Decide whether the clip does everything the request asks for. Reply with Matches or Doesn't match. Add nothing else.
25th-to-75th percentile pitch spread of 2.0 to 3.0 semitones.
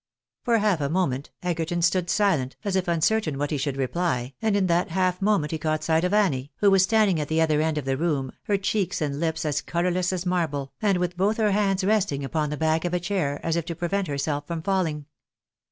Doesn't match